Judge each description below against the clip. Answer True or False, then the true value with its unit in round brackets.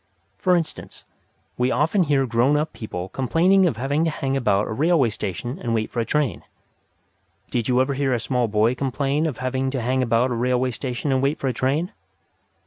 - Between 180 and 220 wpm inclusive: True (205 wpm)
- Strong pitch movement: False (3.3 semitones)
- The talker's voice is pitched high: False (130 Hz)